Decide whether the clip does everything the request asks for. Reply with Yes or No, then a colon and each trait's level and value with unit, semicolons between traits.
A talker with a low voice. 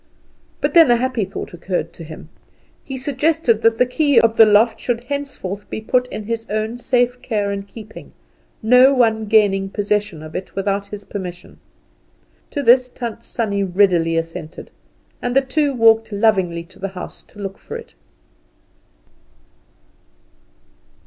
No: high, 220 Hz